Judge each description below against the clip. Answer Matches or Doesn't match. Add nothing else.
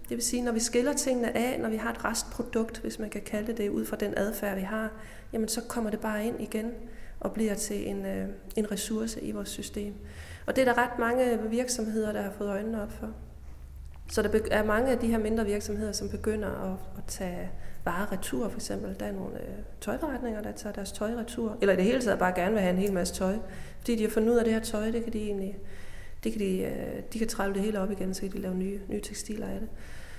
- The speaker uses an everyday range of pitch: Matches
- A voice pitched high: Matches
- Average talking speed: Doesn't match